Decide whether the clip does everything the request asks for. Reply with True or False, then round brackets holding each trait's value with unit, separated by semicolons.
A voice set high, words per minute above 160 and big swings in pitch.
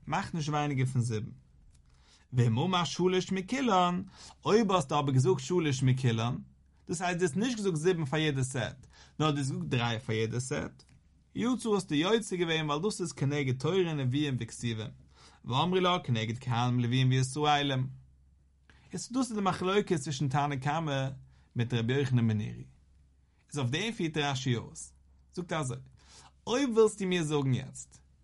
False (140 Hz; 185 wpm; 7.6 semitones)